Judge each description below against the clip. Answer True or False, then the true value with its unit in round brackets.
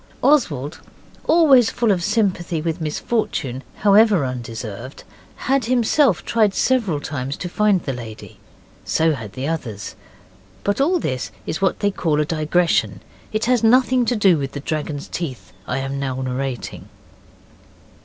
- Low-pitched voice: False (165 Hz)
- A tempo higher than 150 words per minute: False (145 wpm)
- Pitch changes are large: True (8.3 semitones)